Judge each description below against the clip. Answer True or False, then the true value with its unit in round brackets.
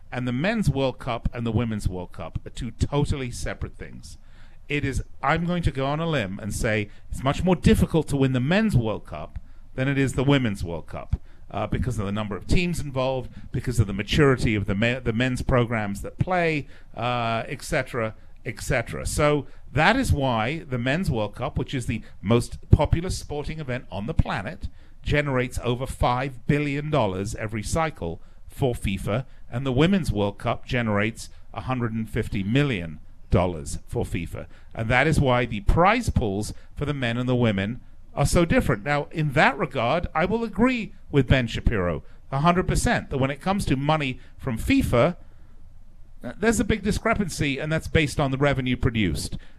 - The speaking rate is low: False (185 wpm)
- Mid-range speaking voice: False (125 Hz)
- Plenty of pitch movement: True (5.8 semitones)